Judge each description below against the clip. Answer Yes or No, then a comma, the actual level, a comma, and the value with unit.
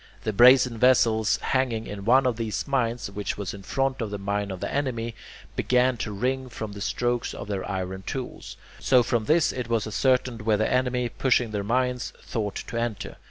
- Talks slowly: No, average, 200 wpm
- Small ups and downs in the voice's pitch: No, average, 3.4 semitones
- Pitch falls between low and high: No, low, 115 Hz